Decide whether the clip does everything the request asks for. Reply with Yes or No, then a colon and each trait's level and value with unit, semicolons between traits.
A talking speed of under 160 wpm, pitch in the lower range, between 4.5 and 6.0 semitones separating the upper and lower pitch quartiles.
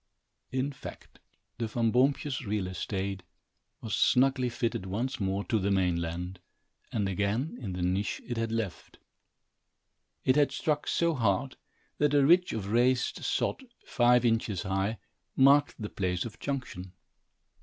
Yes: average, 145 wpm; low, 115 Hz; average, 5.2 semitones